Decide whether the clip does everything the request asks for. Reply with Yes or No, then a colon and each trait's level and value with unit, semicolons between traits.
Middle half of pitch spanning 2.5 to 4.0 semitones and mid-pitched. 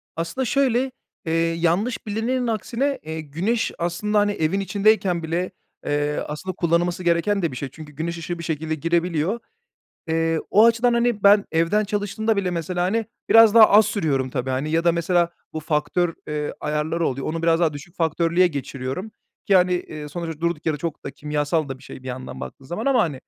No: average, 4.8 semitones; medium, 170 Hz